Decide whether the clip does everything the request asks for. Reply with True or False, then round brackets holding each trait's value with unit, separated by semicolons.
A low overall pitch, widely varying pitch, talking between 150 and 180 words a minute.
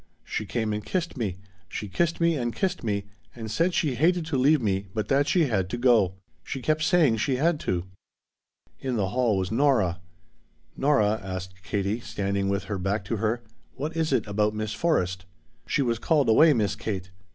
False (115 Hz; 6.3 semitones; 195 wpm)